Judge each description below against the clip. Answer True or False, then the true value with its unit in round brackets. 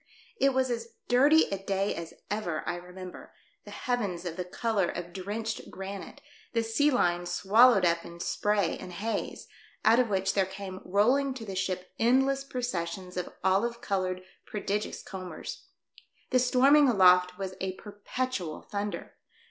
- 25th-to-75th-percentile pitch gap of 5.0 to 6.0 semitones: False (4.5 semitones)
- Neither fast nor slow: True (155 wpm)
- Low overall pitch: False (200 Hz)